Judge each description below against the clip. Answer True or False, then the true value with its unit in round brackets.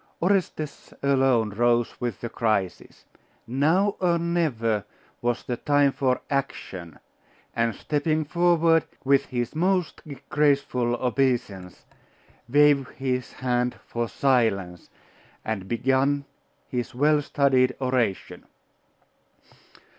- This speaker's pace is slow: True (100 wpm)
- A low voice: True (130 Hz)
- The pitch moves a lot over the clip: False (3.8 semitones)